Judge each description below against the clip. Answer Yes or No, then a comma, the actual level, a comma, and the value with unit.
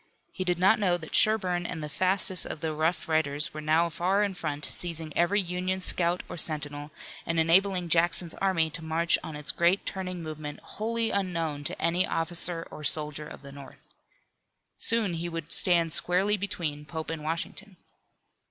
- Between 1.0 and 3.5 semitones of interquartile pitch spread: Yes, average, 2.8 semitones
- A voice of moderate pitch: Yes, medium, 170 Hz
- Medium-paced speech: Yes, average, 175 wpm